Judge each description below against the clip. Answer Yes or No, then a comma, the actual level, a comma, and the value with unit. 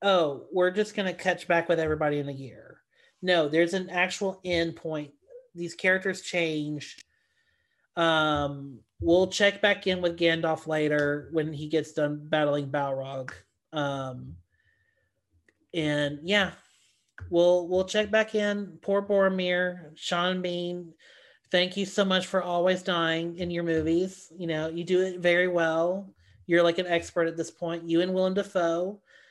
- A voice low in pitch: No, medium, 175 Hz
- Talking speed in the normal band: Yes, average, 155 wpm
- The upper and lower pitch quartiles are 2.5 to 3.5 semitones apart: Yes, average, 3.2 semitones